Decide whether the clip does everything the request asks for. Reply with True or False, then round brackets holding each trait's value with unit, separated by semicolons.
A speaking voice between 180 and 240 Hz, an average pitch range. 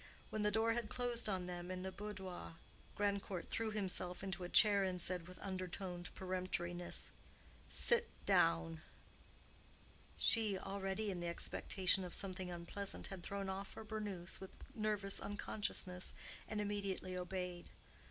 False (190 Hz; 2.3 semitones)